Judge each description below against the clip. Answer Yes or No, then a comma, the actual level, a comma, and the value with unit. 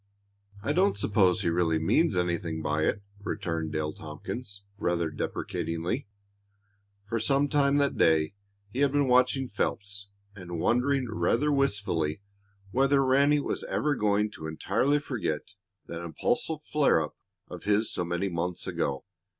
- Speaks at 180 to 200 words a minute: No, average, 140 wpm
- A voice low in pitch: Yes, low, 100 Hz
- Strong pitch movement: Yes, wide, 8.5 semitones